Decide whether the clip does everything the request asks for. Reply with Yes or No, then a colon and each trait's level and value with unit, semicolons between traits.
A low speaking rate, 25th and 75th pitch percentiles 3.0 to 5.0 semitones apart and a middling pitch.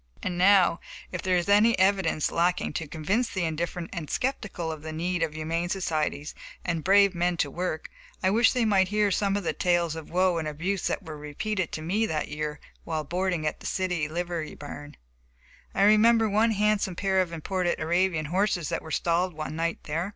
No: average, 200 wpm; average, 3.5 semitones; medium, 175 Hz